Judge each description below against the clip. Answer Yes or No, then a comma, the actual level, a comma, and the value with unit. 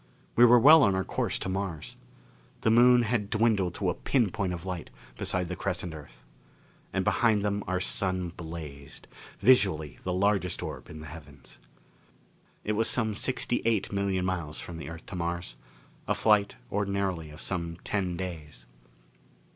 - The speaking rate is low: No, average, 165 wpm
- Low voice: Yes, very low, 95 Hz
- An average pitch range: Yes, average, 3.7 semitones